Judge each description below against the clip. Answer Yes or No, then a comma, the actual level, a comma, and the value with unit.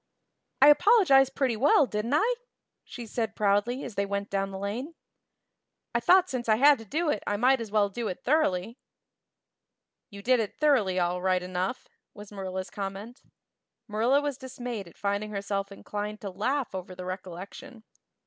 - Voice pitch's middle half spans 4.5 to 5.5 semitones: Yes, average, 4.8 semitones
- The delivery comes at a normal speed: Yes, average, 170 wpm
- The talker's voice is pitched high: Yes, high, 215 Hz